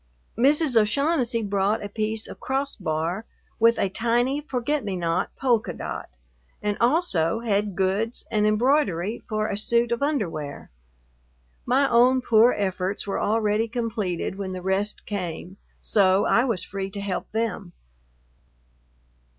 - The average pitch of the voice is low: No, high, 215 Hz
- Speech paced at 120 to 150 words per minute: Yes, slow, 135 wpm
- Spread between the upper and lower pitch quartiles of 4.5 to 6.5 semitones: No, average, 3.7 semitones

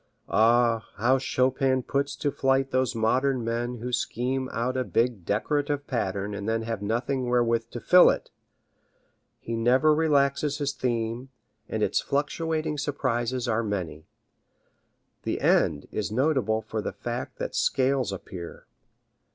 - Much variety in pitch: No, average, 3.1 semitones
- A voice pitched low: Yes, low, 125 Hz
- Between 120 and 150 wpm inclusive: Yes, average, 140 wpm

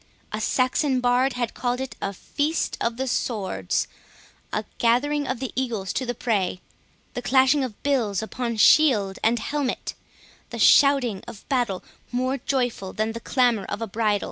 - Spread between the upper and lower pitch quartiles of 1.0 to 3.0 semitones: No, average, 3.4 semitones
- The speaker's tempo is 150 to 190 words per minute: Yes, average, 155 wpm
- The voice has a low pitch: No, high, 245 Hz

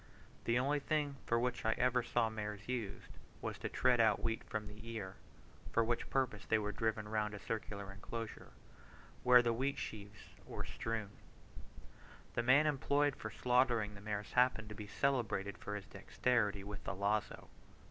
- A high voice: No, low, 115 Hz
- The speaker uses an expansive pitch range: No, average, 3.2 semitones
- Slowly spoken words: No, average, 170 wpm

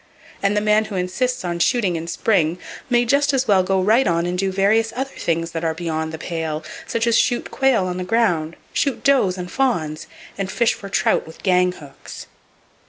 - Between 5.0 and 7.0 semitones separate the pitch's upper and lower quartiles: Yes, average, 5.3 semitones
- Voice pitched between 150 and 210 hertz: Yes, high, 190 Hz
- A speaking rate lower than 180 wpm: No, fast, 205 wpm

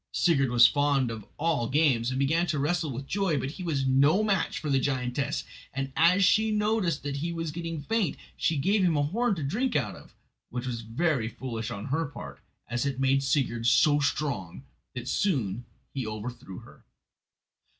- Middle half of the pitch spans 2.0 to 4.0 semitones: No, average, 5.2 semitones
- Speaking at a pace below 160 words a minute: No, average, 190 wpm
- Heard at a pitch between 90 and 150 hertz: Yes, medium, 140 Hz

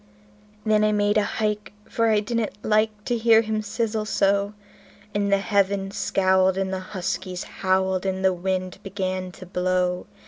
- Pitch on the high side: Yes, high, 200 Hz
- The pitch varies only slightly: Yes, narrow, 2.2 semitones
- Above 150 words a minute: Yes, average, 165 wpm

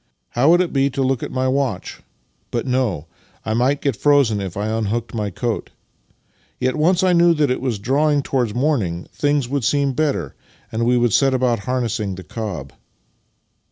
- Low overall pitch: Yes, low, 125 Hz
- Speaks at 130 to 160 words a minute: No, average, 190 wpm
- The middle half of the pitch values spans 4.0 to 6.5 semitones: Yes, average, 4.3 semitones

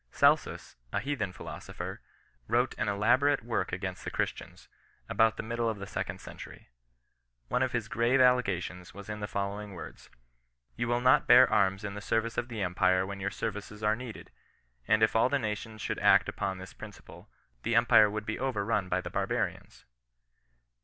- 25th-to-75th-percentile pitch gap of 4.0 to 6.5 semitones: No, average, 3.1 semitones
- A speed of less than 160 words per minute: No, average, 185 wpm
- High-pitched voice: No, low, 105 Hz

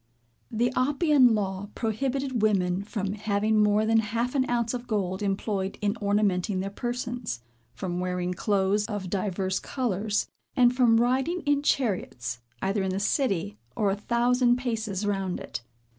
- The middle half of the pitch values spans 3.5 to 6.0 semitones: Yes, average, 4.0 semitones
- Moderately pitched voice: No, high, 210 Hz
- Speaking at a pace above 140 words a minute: Yes, average, 150 wpm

